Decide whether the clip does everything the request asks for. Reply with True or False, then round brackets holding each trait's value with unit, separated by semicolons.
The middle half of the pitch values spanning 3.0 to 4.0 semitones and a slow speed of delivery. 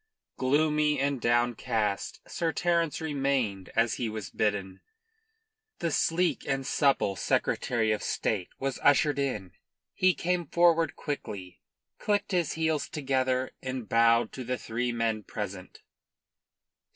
False (5.4 semitones; 125 wpm)